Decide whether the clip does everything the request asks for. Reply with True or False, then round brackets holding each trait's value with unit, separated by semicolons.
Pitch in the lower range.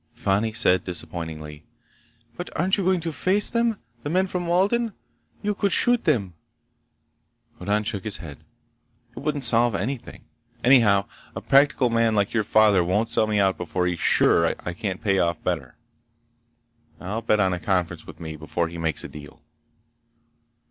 True (105 Hz)